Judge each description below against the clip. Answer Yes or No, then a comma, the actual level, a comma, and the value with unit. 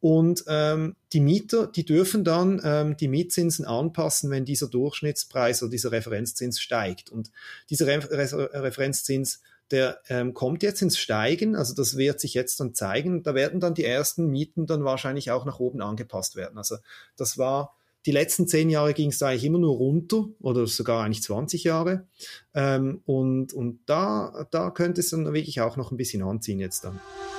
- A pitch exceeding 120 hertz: Yes, medium, 140 Hz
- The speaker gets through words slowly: No, average, 185 wpm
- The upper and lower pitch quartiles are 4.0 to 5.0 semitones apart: Yes, average, 4.5 semitones